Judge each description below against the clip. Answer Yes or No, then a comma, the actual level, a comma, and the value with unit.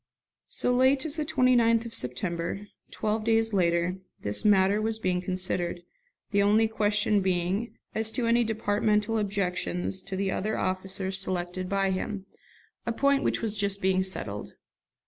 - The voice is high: Yes, high, 200 Hz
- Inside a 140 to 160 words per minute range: Yes, average, 150 wpm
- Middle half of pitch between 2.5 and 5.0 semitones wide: Yes, average, 3.1 semitones